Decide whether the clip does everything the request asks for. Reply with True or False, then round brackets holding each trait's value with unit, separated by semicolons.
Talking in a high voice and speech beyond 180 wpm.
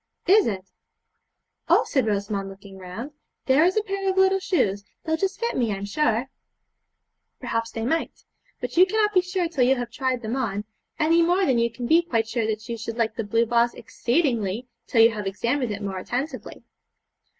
True (240 Hz; 195 wpm)